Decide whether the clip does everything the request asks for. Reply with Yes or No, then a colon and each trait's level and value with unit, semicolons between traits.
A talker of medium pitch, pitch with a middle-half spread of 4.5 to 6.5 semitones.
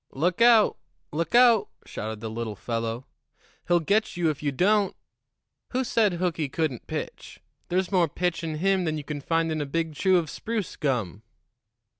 Yes: medium, 165 Hz; average, 5.0 semitones